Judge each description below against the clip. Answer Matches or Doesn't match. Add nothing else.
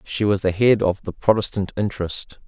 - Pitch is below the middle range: Matches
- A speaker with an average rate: Matches